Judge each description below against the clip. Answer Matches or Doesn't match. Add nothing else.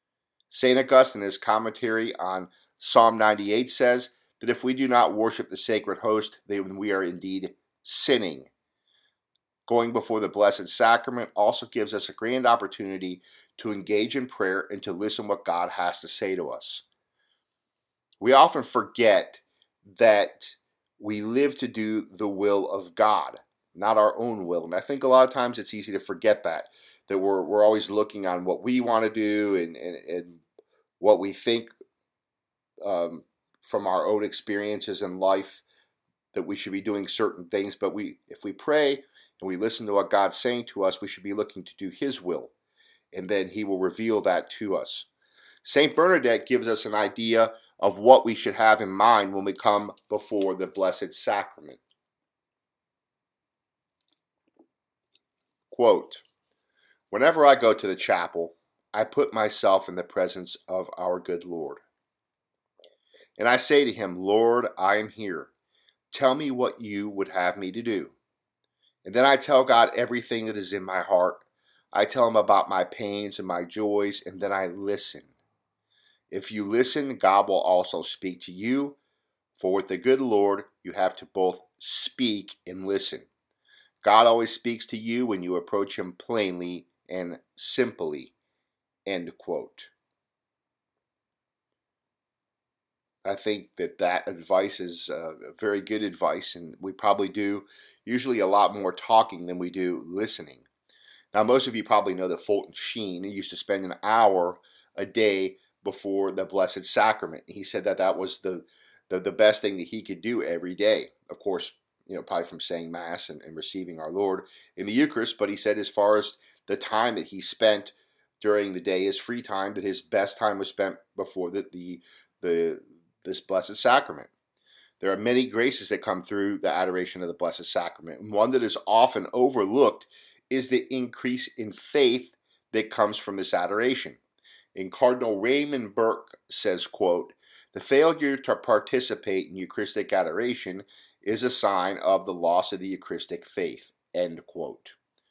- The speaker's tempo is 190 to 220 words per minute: Doesn't match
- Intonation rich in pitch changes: Doesn't match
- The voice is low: Matches